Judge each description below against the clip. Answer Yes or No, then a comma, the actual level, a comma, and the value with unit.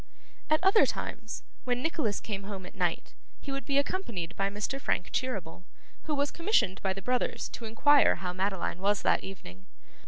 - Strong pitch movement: Yes, wide, 6.5 semitones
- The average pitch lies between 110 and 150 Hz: No, high, 210 Hz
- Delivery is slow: No, average, 180 wpm